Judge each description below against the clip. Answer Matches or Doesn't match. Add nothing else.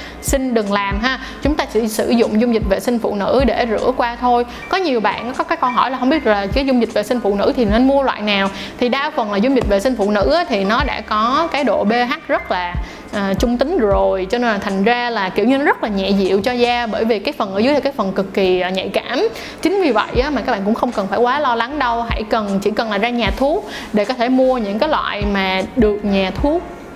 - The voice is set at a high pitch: Matches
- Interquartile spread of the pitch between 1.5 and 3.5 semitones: Doesn't match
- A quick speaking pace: Matches